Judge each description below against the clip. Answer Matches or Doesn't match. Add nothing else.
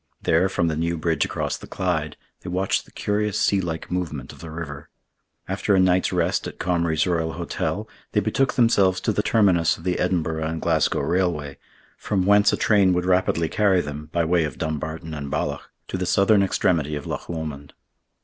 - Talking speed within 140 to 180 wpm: Doesn't match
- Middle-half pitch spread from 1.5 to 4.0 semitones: Matches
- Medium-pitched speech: Doesn't match